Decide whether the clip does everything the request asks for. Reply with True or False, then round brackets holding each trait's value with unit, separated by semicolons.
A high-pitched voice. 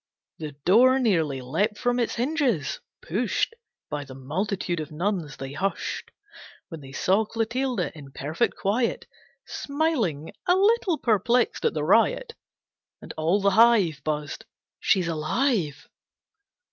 True (195 Hz)